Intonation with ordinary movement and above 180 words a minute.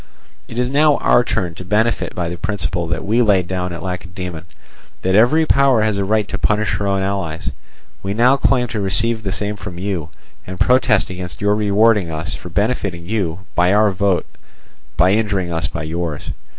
Yes: average, 3.5 semitones; average, 190 wpm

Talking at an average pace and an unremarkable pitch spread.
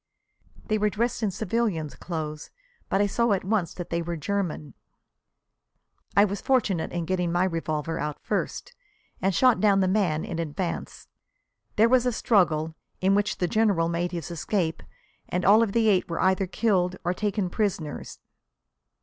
Yes: average, 165 wpm; average, 3.9 semitones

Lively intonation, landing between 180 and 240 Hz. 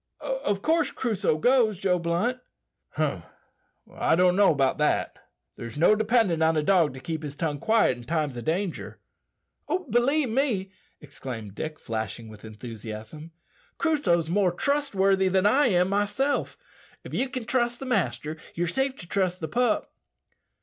Yes: wide, 7.8 semitones; medium, 185 Hz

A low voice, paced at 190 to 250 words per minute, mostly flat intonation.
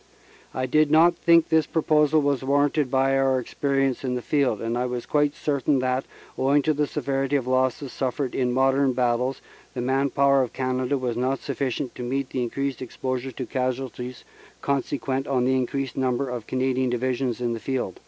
Yes: low, 130 Hz; average, 195 wpm; narrow, 1.7 semitones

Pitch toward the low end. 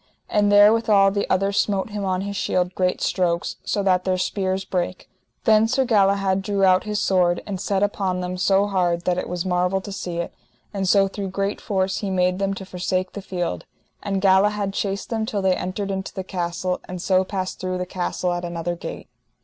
No: high, 190 Hz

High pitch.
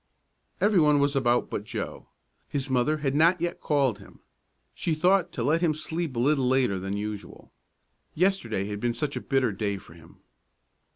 No: low, 135 Hz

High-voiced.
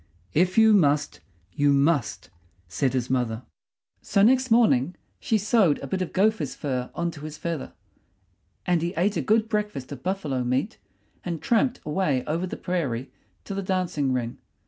No: medium, 170 Hz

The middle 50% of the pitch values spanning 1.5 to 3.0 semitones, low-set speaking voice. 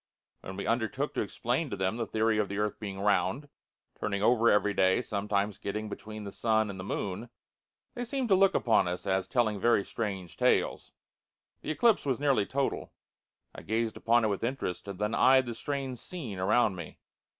No: average, 3.9 semitones; low, 110 Hz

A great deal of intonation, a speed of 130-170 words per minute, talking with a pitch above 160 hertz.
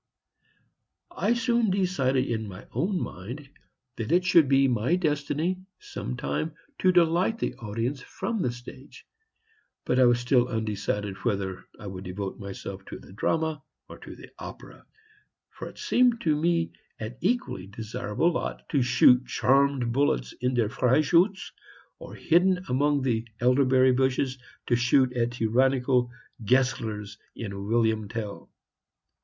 No: wide, 6.1 semitones; average, 140 wpm; low, 130 Hz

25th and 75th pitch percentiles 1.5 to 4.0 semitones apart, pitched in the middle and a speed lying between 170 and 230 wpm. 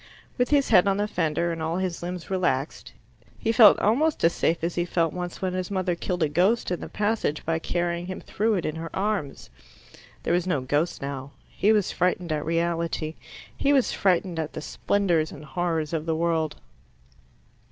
Yes: average, 2.9 semitones; medium, 175 Hz; average, 195 wpm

